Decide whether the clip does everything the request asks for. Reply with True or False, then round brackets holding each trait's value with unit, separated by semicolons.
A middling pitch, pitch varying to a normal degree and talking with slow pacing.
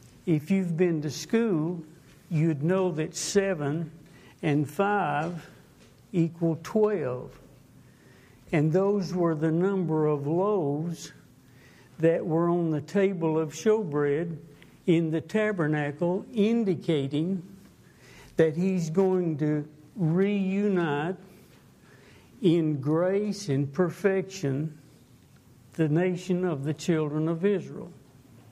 True (165 Hz; 3.7 semitones; 100 wpm)